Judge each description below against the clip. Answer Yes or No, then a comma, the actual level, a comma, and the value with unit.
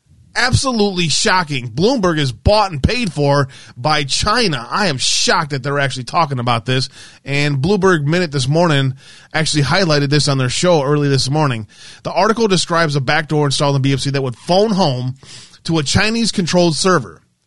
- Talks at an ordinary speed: Yes, average, 170 wpm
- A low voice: No, medium, 150 Hz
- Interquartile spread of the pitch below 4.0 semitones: No, average, 4.3 semitones